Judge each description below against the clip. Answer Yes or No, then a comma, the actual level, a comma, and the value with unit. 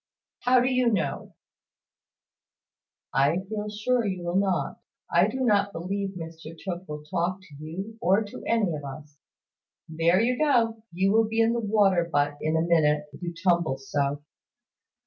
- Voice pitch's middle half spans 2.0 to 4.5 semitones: No, average, 5.2 semitones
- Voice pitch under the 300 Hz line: Yes, medium, 185 Hz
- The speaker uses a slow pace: No, average, 165 wpm